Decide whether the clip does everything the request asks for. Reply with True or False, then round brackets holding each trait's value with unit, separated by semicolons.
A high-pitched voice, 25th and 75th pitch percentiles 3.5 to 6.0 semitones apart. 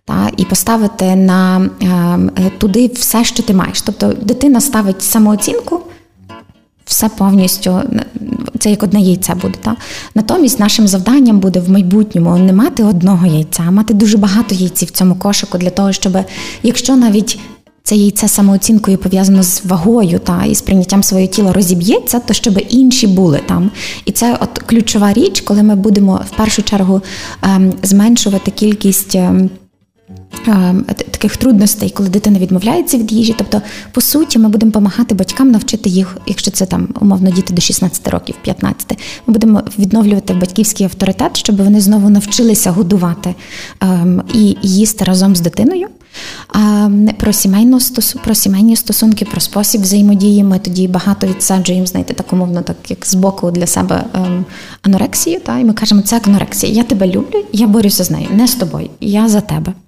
False (205 Hz; 2.8 semitones)